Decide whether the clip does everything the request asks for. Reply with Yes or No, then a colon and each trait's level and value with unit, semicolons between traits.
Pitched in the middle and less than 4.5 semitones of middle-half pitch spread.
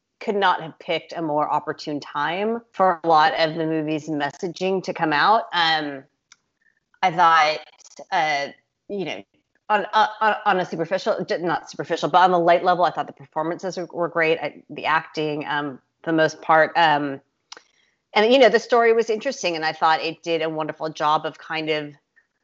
Yes: medium, 165 Hz; average, 3.4 semitones